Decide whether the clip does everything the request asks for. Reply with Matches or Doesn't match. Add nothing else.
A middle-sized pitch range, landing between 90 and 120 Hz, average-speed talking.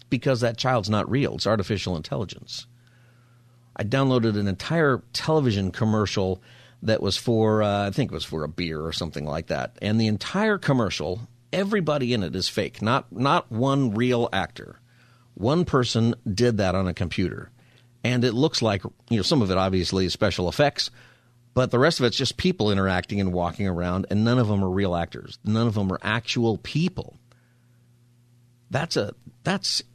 Matches